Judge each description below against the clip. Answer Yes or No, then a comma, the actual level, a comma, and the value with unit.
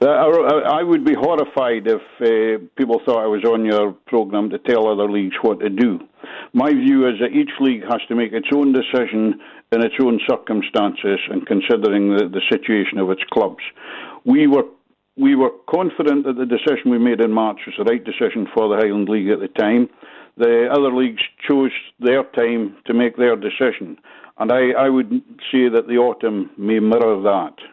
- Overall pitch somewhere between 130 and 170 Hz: No, low, 120 Hz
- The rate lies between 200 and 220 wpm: No, average, 190 wpm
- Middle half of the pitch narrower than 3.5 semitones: No, average, 4.5 semitones